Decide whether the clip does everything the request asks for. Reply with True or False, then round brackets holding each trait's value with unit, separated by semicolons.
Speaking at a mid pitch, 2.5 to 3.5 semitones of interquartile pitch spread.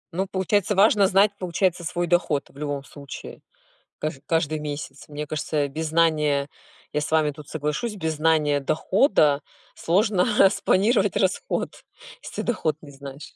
False (160 Hz; 4.3 semitones)